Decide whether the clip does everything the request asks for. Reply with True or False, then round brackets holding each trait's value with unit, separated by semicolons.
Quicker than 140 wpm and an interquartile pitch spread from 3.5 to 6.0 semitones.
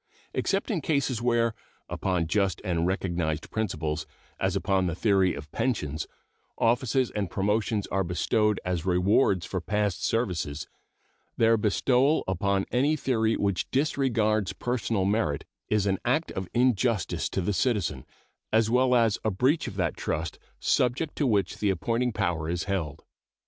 True (150 wpm; 4.9 semitones)